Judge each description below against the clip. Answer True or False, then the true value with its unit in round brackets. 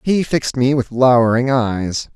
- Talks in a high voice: False (125 Hz)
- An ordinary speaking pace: True (165 wpm)